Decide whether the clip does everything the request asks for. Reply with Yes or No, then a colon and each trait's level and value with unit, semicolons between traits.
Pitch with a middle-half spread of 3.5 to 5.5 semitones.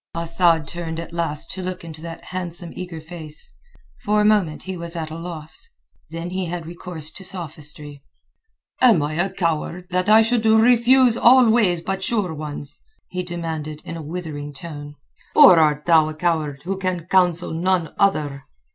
No: average, 3.1 semitones